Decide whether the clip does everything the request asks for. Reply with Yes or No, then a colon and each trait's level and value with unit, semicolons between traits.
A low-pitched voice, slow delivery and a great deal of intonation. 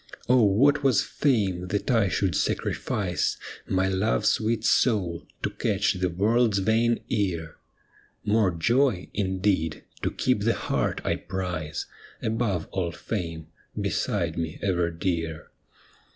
No: very low, 95 Hz; slow, 130 wpm; average, 4.2 semitones